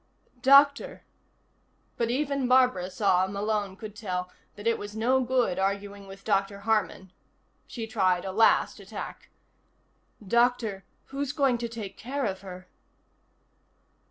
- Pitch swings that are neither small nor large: Yes, average, 4.2 semitones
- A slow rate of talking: Yes, slow, 130 wpm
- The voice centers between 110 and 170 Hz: No, high, 215 Hz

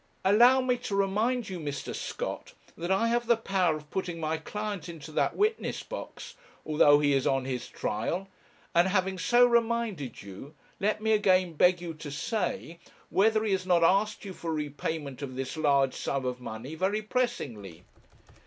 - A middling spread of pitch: No, wide, 6.6 semitones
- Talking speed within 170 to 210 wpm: Yes, average, 175 wpm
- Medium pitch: Yes, medium, 180 Hz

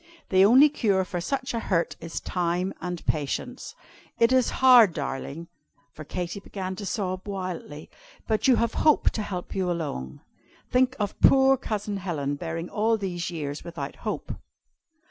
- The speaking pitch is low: No, medium, 185 Hz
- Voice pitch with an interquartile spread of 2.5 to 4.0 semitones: No, average, 4.9 semitones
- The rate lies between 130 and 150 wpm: No, average, 160 wpm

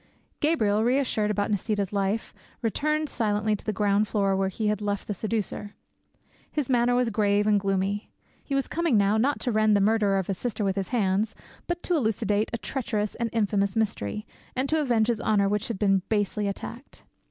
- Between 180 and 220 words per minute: Yes, average, 195 wpm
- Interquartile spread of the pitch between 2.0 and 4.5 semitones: Yes, narrow, 2.6 semitones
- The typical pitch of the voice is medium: No, high, 210 Hz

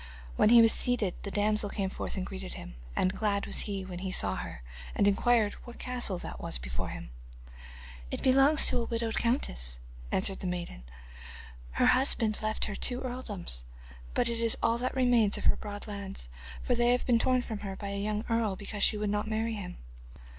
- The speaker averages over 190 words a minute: Yes, fast, 205 wpm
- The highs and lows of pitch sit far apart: No, average, 3.4 semitones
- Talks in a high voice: Yes, high, 210 Hz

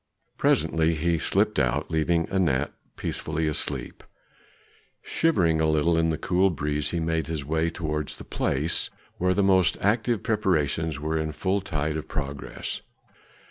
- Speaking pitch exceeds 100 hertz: No, very low, 80 Hz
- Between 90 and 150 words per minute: Yes, average, 145 wpm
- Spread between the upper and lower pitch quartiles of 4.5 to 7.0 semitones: No, narrow, 2.6 semitones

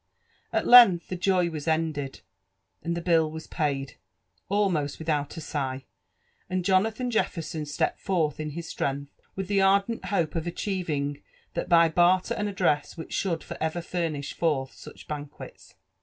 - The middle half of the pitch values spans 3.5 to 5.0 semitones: Yes, average, 3.9 semitones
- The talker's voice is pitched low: No, medium, 165 Hz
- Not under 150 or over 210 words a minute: Yes, average, 160 wpm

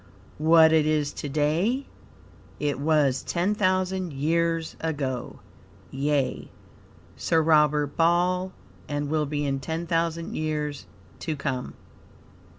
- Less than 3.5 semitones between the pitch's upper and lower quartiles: Yes, narrow, 2.5 semitones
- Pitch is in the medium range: Yes, medium, 155 Hz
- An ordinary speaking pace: No, slow, 115 wpm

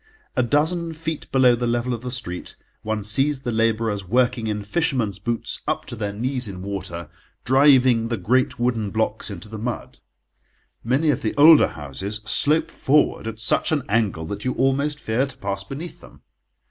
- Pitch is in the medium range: No, low, 120 Hz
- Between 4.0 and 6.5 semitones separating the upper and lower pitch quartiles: Yes, average, 4.3 semitones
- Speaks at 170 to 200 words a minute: Yes, average, 180 wpm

